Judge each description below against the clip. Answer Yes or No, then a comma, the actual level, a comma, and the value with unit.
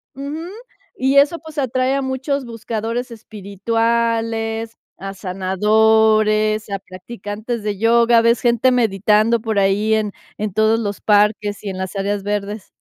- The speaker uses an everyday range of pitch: No, narrow, 2.3 semitones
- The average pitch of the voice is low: No, high, 220 Hz